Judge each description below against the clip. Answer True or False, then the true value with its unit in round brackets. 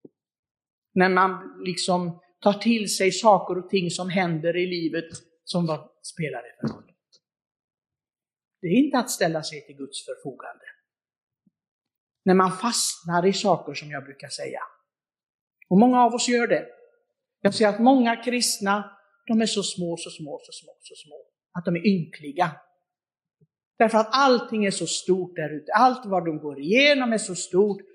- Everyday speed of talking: True (165 wpm)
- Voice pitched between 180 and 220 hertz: True (190 Hz)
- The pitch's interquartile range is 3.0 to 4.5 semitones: False (5.3 semitones)